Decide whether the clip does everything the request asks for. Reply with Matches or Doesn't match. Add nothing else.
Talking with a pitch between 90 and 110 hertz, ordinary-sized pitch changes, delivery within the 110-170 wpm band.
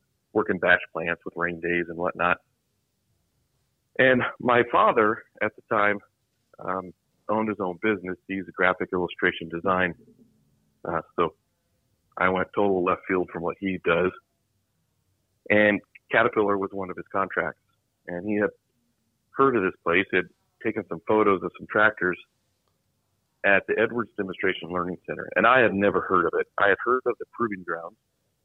Matches